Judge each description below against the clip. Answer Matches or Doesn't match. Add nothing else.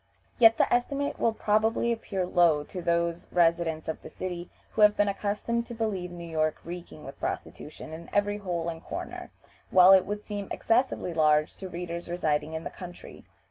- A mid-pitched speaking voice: Matches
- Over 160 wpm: Matches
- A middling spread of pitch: Matches